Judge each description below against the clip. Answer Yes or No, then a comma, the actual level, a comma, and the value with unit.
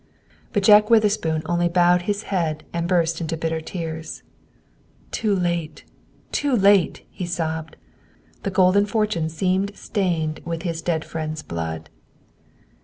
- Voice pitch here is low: No, medium, 175 Hz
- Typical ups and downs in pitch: Yes, average, 3.4 semitones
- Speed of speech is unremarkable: No, slow, 130 wpm